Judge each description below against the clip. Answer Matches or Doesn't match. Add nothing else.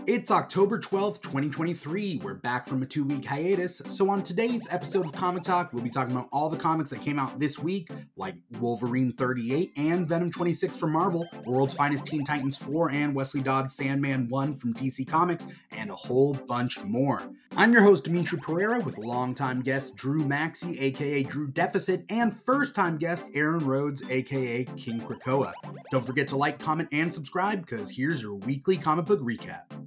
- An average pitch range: Matches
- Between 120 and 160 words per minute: Doesn't match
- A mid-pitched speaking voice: Matches